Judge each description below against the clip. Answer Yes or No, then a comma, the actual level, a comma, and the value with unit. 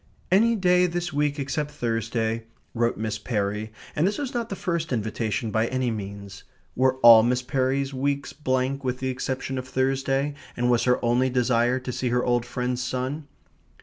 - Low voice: Yes, low, 130 Hz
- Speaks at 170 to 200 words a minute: Yes, average, 180 wpm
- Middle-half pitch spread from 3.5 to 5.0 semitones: No, average, 3.0 semitones